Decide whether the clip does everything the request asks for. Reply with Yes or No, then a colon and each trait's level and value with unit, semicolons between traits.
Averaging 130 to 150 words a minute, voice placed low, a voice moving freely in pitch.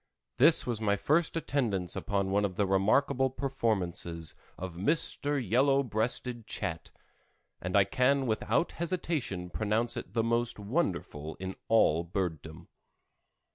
Yes: slow, 135 wpm; low, 110 Hz; wide, 6.0 semitones